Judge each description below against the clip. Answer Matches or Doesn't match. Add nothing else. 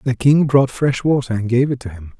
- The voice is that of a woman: Doesn't match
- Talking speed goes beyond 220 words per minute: Matches